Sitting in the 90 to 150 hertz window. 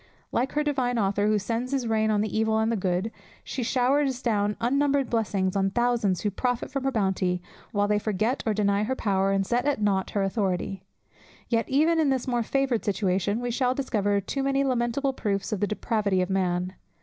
No: high, 220 Hz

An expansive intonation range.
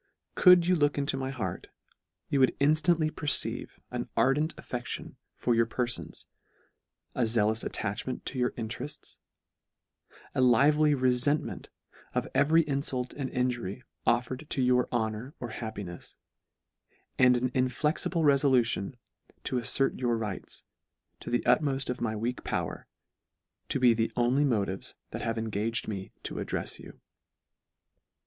No: average, 3.4 semitones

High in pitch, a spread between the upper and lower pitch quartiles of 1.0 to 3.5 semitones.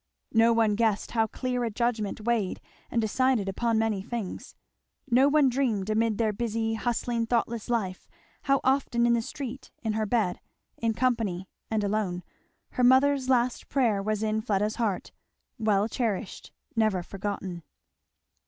Yes: high, 225 Hz; narrow, 2.5 semitones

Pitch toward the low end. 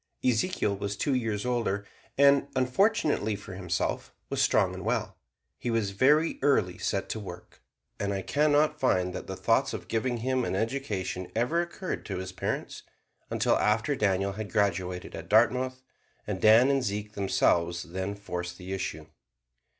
Yes: low, 105 Hz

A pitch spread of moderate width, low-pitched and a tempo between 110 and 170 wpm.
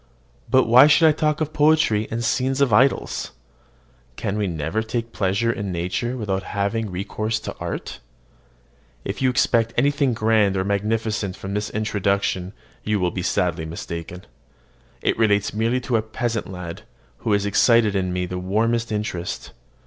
Yes: average, 3.4 semitones; low, 105 Hz; average, 160 wpm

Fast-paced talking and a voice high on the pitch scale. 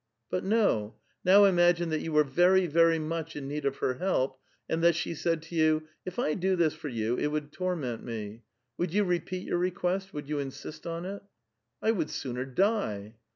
No: fast, 220 wpm; medium, 160 Hz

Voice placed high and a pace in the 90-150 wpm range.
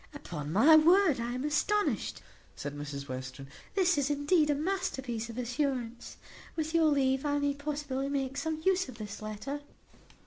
No: very high, 280 Hz; average, 165 wpm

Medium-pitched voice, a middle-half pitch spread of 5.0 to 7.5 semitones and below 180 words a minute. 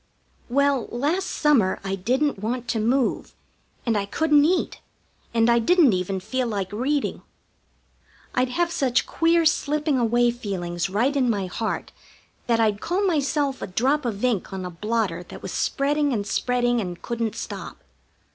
No: high, 240 Hz; wide, 5.5 semitones; average, 160 wpm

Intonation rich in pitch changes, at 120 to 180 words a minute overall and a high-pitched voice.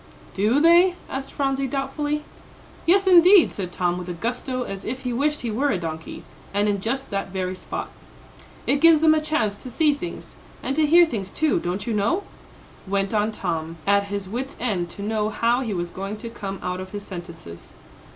No: wide, 6.7 semitones; average, 200 wpm; high, 220 Hz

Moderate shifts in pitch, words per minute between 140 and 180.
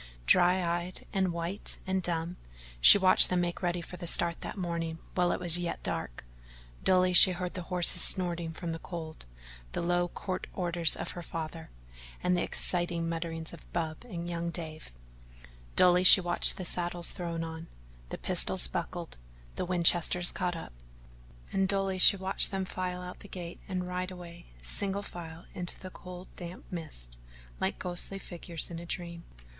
No: narrow, 1.4 semitones; average, 170 wpm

